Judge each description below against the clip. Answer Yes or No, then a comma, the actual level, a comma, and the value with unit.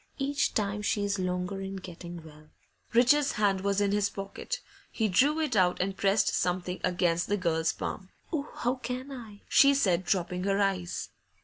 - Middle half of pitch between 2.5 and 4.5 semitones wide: Yes, average, 3.5 semitones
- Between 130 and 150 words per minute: No, average, 175 wpm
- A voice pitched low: No, high, 195 Hz